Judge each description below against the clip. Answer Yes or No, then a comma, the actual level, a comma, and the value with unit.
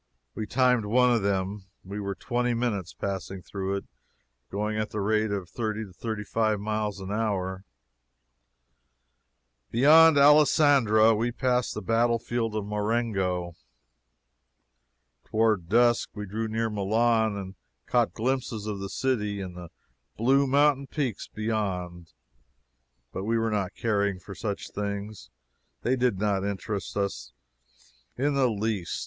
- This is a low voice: Yes, low, 110 Hz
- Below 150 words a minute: Yes, average, 140 wpm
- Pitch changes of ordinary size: Yes, average, 3.1 semitones